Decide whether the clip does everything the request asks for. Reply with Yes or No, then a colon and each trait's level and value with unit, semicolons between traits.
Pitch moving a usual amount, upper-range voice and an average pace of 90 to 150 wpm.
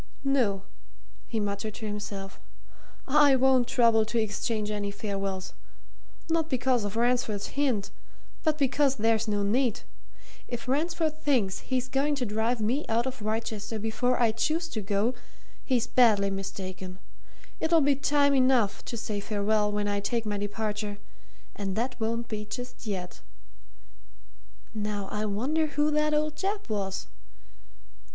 Yes: average, 4.3 semitones; high, 225 Hz; average, 145 wpm